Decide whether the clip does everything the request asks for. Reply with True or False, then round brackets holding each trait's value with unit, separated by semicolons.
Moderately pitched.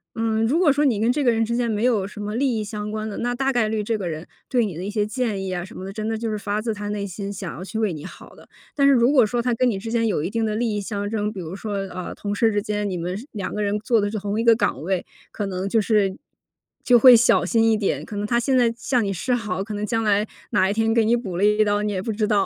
False (215 Hz)